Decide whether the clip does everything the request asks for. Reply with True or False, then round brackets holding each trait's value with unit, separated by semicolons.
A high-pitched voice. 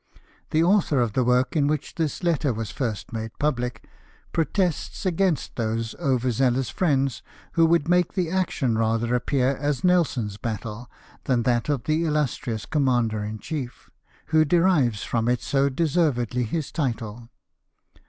False (130 Hz)